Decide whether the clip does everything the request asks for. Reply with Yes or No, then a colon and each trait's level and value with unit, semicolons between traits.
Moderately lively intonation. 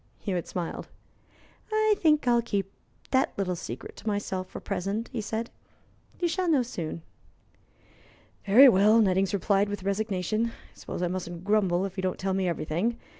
Yes: average, 3.8 semitones